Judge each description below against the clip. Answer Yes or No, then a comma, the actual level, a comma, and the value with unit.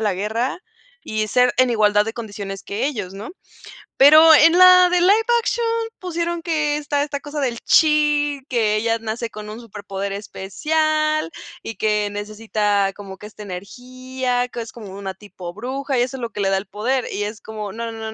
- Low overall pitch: No, high, 230 Hz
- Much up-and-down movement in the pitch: Yes, wide, 5.9 semitones